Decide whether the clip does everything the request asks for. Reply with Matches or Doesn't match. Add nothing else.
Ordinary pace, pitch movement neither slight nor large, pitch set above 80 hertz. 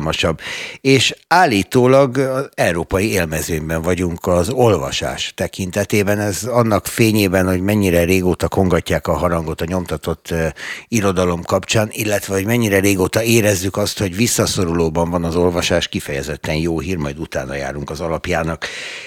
Matches